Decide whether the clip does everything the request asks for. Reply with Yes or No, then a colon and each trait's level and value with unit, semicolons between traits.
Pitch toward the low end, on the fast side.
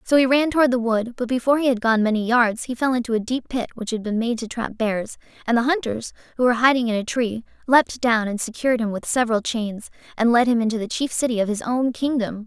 No: high, 235 Hz; fast, 260 wpm